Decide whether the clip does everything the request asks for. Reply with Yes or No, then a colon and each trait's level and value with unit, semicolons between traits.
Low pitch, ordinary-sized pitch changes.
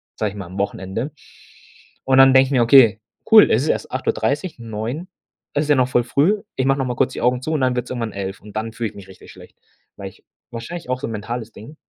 Yes: low, 125 Hz; average, 4.0 semitones